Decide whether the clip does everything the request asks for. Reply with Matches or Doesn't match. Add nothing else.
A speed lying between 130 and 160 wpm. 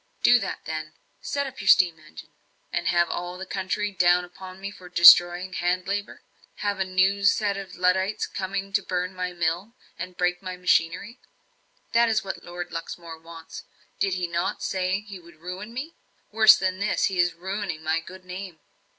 Doesn't match